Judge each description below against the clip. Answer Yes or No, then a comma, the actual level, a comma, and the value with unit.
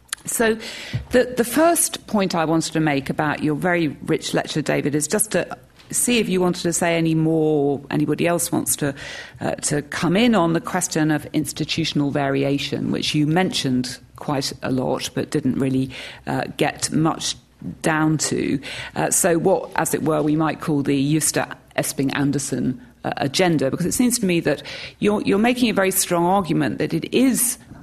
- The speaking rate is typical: Yes, average, 185 wpm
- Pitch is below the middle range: No, medium, 155 Hz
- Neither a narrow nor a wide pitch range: Yes, average, 4.3 semitones